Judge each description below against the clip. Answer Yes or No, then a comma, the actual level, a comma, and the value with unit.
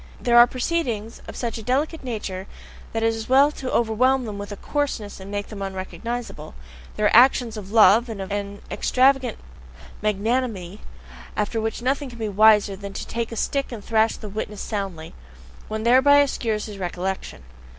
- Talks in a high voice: Yes, high, 220 Hz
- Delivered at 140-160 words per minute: No, average, 175 wpm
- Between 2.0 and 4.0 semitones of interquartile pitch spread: Yes, average, 3.5 semitones